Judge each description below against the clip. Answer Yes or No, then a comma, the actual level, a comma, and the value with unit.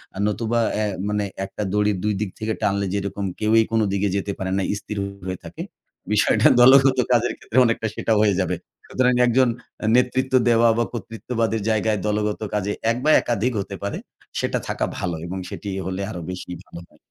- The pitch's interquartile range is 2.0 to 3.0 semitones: Yes, narrow, 2.6 semitones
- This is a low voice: Yes, low, 110 Hz